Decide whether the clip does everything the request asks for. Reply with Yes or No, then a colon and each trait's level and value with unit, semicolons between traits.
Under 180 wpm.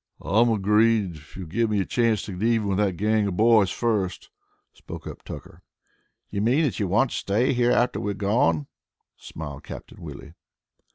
No: average, 185 wpm